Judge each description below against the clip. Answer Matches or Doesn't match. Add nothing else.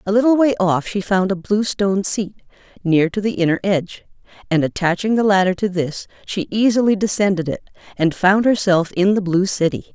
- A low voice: Doesn't match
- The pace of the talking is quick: Doesn't match